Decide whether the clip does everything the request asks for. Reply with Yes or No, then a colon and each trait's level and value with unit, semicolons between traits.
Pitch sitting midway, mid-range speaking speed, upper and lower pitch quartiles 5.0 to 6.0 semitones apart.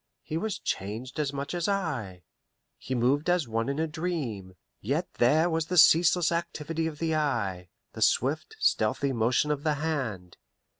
Yes: medium, 150 Hz; average, 165 wpm; wide, 5.4 semitones